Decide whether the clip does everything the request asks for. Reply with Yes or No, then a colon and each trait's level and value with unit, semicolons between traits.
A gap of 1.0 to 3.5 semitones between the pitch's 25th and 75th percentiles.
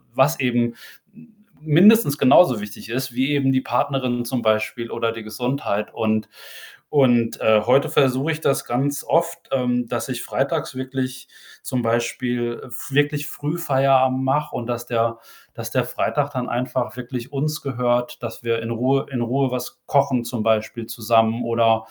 Yes: average, 2.7 semitones